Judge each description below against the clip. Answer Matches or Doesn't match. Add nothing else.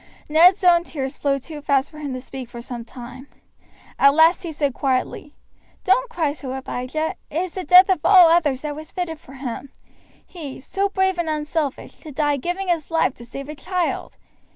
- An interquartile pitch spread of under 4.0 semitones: Doesn't match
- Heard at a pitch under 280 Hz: Doesn't match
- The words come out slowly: Doesn't match